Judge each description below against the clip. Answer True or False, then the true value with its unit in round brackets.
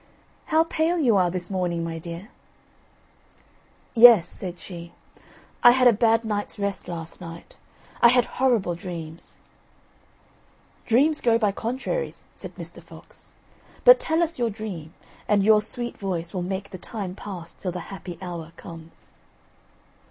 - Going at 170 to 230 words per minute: False (145 wpm)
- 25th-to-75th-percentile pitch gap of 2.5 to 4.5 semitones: False (5.4 semitones)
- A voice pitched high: True (200 Hz)